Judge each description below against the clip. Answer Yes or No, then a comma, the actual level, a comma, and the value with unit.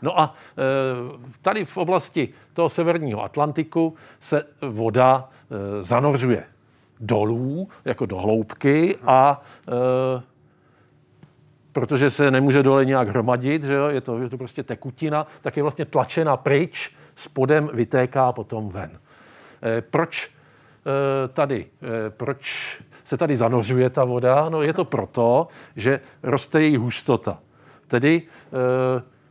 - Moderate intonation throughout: Yes, average, 3.3 semitones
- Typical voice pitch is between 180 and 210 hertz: No, low, 135 Hz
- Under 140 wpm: Yes, average, 130 wpm